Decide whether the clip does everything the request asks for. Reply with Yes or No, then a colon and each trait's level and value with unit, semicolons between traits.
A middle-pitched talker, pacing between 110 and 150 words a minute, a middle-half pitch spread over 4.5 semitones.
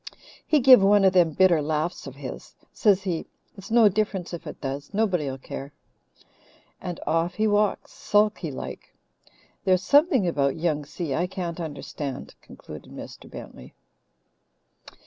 Yes: medium, 175 Hz; average, 145 wpm; average, 5.3 semitones